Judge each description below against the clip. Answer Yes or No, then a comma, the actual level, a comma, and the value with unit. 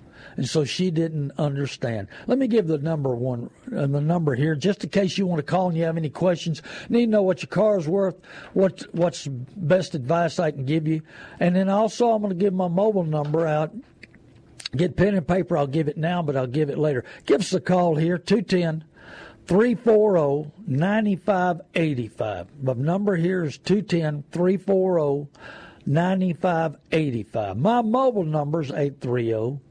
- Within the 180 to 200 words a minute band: No, average, 165 wpm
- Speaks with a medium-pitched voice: Yes, medium, 170 Hz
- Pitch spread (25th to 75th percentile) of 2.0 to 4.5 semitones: Yes, average, 4.2 semitones